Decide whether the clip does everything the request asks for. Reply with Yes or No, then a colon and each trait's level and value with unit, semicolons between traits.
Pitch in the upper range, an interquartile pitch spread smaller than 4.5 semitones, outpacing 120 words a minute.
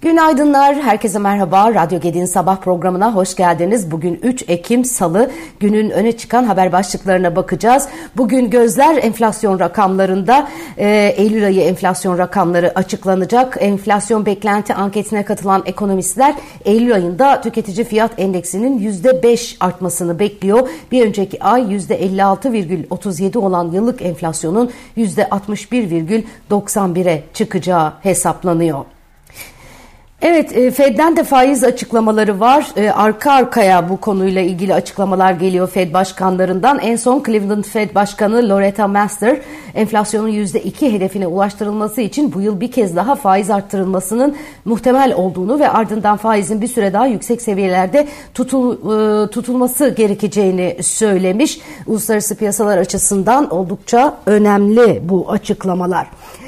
No: high, 210 Hz; average, 4.1 semitones; average, 115 wpm